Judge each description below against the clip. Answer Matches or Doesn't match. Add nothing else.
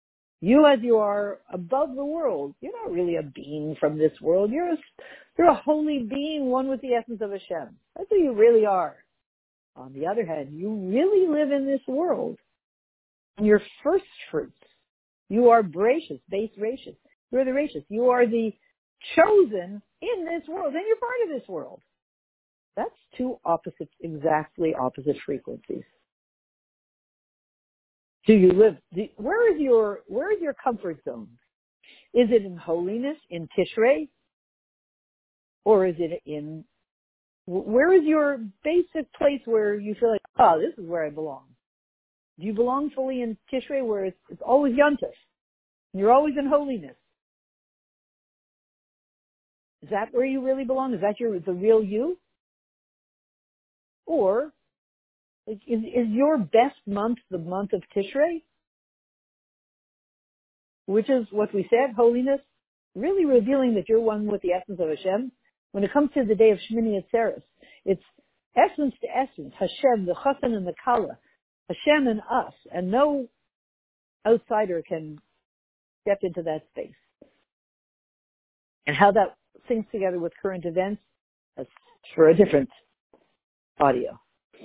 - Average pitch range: Doesn't match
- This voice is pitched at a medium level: Doesn't match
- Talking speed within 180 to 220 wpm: Doesn't match